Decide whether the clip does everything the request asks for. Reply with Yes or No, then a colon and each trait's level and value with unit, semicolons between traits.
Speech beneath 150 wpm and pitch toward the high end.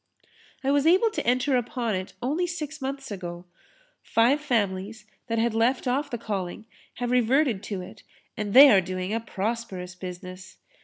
No: average, 165 wpm; high, 230 Hz